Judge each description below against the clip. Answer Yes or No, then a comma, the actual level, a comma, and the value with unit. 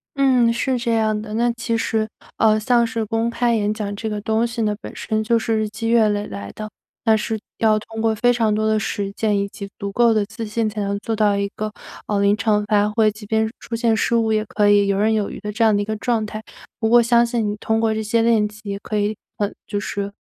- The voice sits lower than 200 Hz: No, high, 220 Hz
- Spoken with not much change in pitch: Yes, narrow, 1.5 semitones